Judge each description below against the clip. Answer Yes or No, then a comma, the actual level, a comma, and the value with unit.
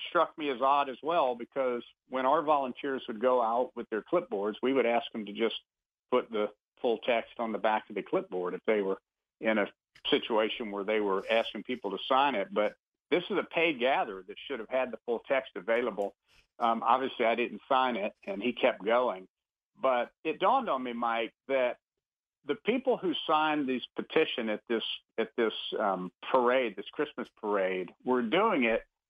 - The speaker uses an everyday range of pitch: Yes, average, 4.0 semitones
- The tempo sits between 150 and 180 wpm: No, average, 195 wpm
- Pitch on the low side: Yes, low, 120 Hz